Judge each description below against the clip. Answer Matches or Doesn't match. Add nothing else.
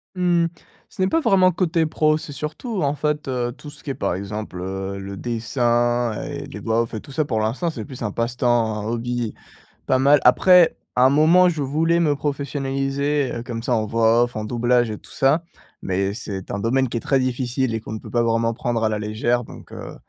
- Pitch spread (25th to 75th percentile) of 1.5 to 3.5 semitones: Doesn't match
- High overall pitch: Doesn't match